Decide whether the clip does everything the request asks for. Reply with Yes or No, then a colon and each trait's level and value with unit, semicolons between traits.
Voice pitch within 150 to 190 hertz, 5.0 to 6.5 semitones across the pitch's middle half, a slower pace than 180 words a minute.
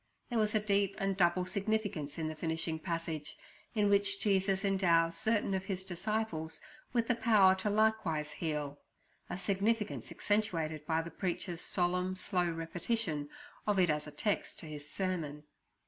No: medium, 185 Hz; average, 4.0 semitones; average, 155 wpm